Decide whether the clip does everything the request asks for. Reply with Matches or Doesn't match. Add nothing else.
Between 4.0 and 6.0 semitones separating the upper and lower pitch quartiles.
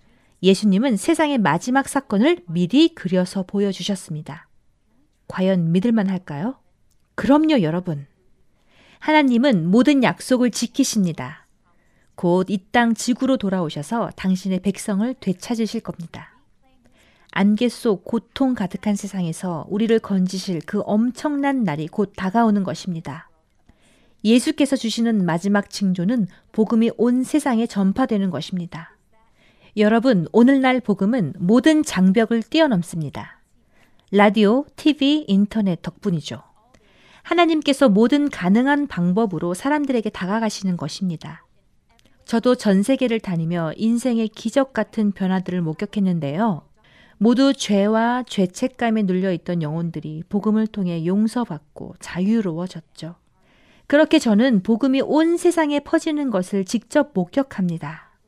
Matches